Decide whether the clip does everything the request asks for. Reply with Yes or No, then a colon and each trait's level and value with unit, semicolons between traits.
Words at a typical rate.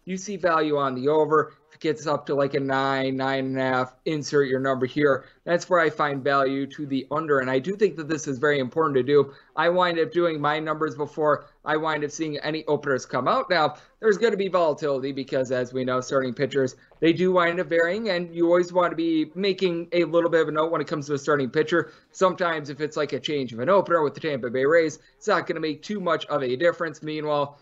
No: fast, 255 wpm